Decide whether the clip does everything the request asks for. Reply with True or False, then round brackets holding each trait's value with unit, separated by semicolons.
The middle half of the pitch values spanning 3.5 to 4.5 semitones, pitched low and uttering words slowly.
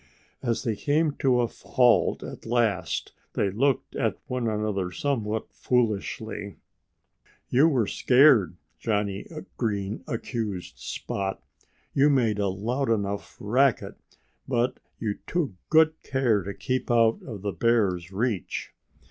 True (4.0 semitones; 115 Hz; 125 wpm)